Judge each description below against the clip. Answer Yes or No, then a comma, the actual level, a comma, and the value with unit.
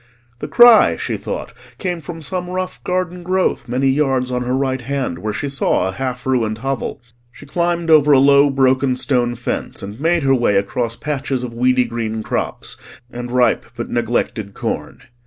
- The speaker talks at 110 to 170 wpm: No, average, 180 wpm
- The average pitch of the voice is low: Yes, low, 130 Hz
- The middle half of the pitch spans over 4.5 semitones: No, average, 3.7 semitones